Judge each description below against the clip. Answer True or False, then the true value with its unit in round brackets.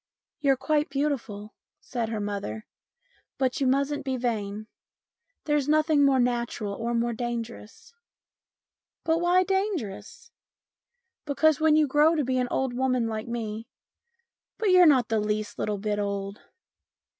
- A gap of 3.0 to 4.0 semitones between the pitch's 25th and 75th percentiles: False (5.5 semitones)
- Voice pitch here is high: True (255 Hz)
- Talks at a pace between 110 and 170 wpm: True (160 wpm)